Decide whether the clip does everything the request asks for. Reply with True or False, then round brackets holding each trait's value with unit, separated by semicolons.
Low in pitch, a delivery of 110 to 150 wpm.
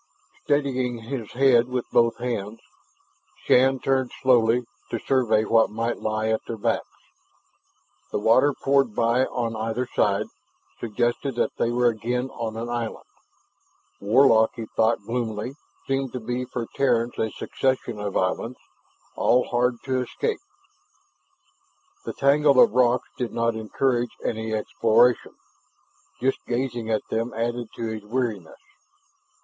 True (120 Hz; 135 wpm)